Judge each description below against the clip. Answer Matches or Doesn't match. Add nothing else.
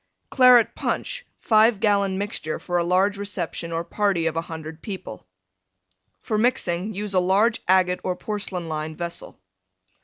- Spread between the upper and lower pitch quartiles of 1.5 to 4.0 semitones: Matches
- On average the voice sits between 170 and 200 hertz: Matches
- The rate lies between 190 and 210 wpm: Doesn't match